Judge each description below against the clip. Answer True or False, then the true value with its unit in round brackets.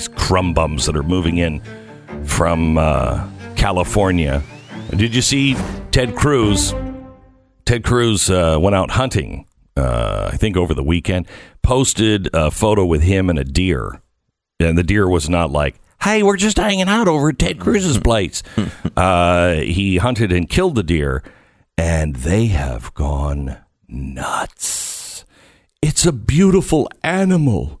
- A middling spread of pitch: False (6.1 semitones)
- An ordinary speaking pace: True (145 wpm)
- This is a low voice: True (90 Hz)